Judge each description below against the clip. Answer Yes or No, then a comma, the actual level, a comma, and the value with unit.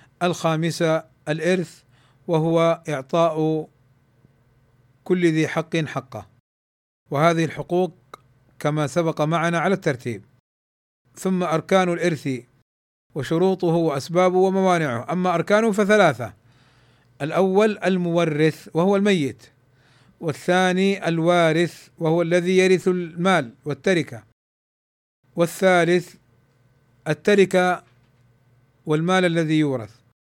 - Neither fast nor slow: Yes, average, 80 wpm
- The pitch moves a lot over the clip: Yes, wide, 5.8 semitones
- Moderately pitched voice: Yes, medium, 160 Hz